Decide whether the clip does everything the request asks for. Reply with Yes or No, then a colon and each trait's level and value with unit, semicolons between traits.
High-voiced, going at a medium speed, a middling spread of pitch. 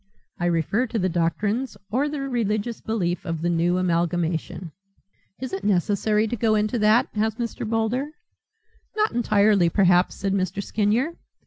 Yes: high, 210 Hz; average, 150 wpm; average, 4.2 semitones